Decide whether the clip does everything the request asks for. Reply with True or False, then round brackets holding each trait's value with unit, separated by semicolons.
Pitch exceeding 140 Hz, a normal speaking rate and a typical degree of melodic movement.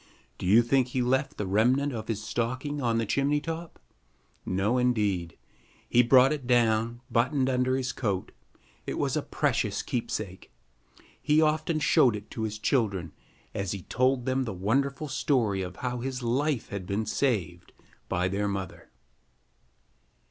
False (120 Hz; 155 wpm; 4.4 semitones)